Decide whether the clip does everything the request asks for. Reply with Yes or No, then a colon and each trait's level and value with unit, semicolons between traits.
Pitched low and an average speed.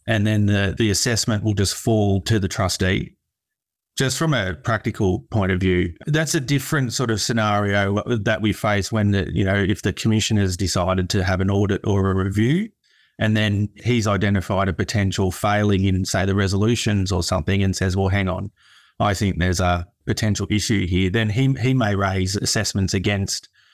Yes: low, 100 Hz; average, 190 wpm